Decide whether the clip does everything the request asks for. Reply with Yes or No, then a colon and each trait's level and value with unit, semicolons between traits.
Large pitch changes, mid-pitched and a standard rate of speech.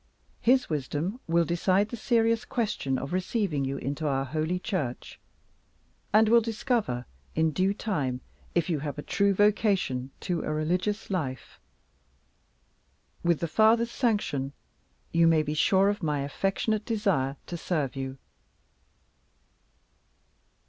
No: wide, 6.3 semitones; medium, 175 Hz; slow, 130 wpm